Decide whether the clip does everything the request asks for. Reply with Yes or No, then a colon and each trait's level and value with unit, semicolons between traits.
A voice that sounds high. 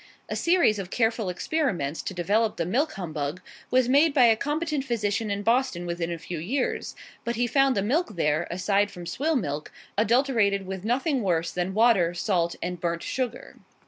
Yes: high, 205 Hz